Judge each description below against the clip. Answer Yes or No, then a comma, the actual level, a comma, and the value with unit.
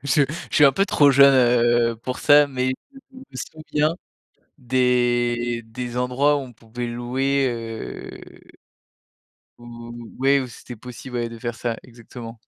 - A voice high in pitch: No, low, 125 Hz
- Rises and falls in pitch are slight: Yes, narrow, 2.3 semitones